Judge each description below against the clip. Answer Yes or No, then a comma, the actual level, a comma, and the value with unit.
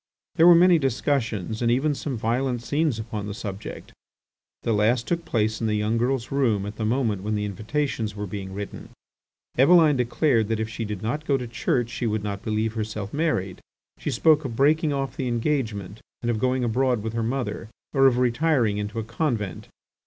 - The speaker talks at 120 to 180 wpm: No, average, 195 wpm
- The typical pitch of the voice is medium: No, low, 115 Hz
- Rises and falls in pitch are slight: No, average, 4.1 semitones